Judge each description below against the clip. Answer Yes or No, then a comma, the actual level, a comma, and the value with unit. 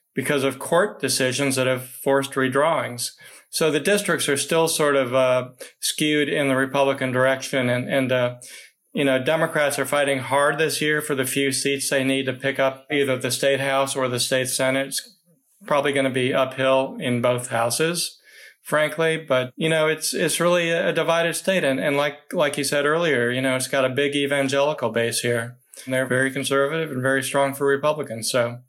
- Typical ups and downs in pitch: No, narrow, 2.3 semitones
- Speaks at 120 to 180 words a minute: No, average, 195 wpm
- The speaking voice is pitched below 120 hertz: No, low, 135 Hz